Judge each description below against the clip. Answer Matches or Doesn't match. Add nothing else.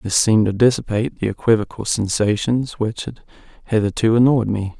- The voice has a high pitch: Doesn't match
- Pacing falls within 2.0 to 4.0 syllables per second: Doesn't match